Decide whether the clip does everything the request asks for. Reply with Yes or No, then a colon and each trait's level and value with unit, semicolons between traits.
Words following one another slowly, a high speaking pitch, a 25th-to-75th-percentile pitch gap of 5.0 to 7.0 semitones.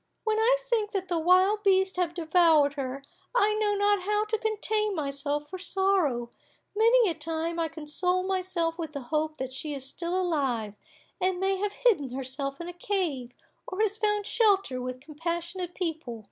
No: average, 175 wpm; very high, 350 Hz; average, 5.3 semitones